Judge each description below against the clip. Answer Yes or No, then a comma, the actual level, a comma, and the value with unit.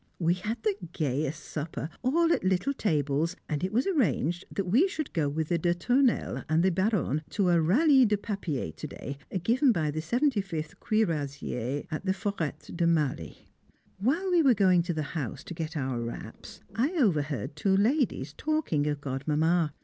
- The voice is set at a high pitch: No, medium, 175 Hz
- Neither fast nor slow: Yes, average, 180 wpm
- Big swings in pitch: Yes, wide, 6.7 semitones